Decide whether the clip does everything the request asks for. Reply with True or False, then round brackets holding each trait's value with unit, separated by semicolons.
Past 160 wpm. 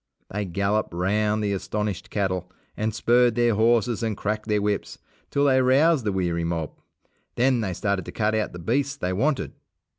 True (180 wpm)